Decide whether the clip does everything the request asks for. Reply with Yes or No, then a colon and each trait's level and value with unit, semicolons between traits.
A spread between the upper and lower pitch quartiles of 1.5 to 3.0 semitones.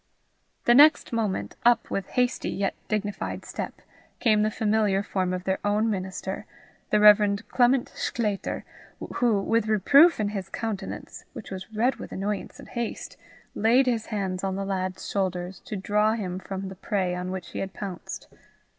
Yes: average, 2.7 semitones